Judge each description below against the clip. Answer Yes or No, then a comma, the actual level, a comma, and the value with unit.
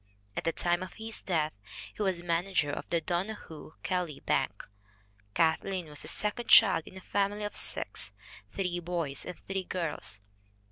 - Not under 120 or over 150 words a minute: No, average, 160 wpm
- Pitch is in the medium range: Yes, medium, 175 Hz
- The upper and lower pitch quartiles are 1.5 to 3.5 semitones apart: Yes, average, 3.1 semitones